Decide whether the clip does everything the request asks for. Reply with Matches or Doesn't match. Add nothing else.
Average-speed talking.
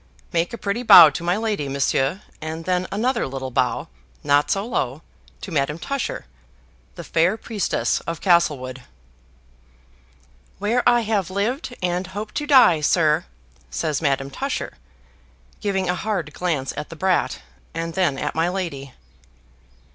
Matches